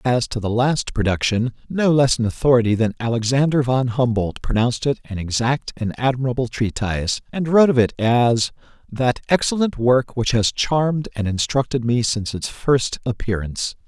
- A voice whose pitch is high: No, low, 120 Hz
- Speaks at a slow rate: No, average, 165 wpm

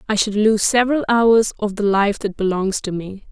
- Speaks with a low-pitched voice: No, high, 210 Hz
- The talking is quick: Yes, fast, 215 wpm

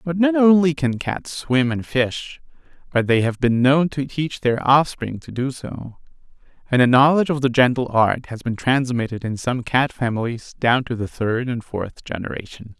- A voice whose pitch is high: No, low, 125 Hz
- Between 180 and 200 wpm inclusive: Yes, average, 190 wpm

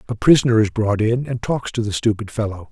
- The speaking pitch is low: Yes, low, 115 Hz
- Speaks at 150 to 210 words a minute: No, fast, 245 wpm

